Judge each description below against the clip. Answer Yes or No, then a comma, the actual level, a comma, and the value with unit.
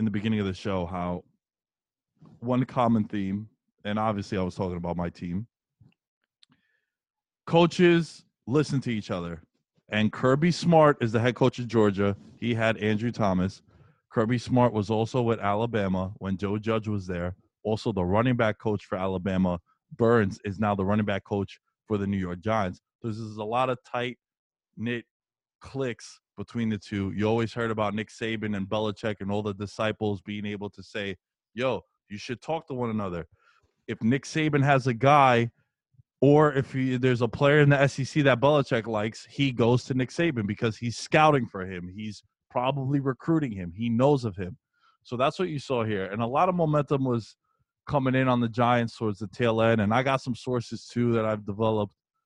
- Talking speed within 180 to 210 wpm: Yes, average, 190 wpm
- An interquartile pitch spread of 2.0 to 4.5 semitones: Yes, average, 3.9 semitones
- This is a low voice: Yes, low, 115 Hz